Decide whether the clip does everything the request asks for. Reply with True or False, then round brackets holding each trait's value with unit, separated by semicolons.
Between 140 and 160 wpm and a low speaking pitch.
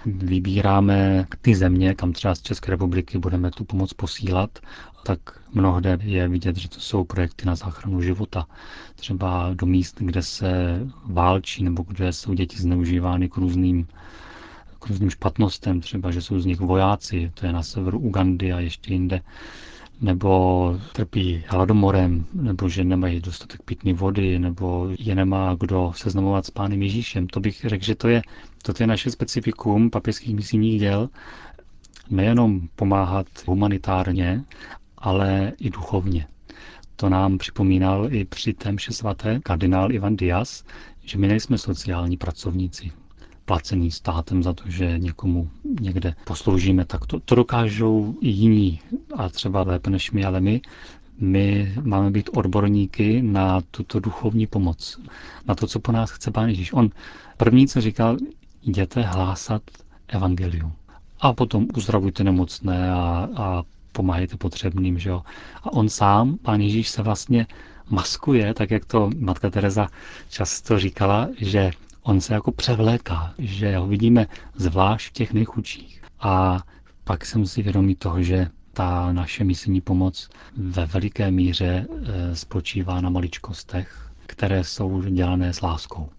True (145 wpm; 95 Hz)